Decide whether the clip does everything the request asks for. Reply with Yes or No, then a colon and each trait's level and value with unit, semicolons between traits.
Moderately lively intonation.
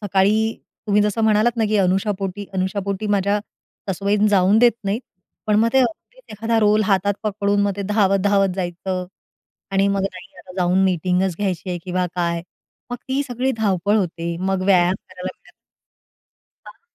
No: narrow, 2.2 semitones